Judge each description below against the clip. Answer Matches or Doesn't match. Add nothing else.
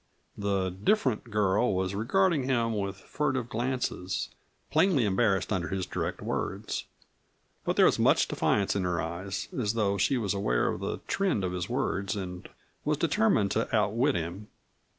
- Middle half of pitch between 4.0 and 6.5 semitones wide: Matches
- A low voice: Matches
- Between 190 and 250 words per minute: Doesn't match